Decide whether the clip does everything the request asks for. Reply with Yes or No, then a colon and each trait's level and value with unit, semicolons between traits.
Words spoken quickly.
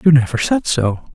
Yes: fast, 210 wpm